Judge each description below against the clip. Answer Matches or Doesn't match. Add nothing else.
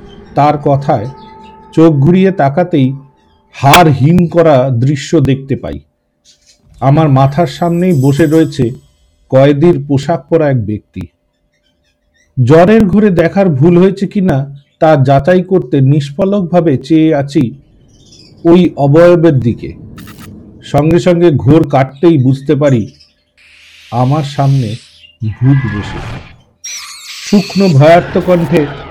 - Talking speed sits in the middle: Matches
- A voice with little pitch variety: Doesn't match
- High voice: Doesn't match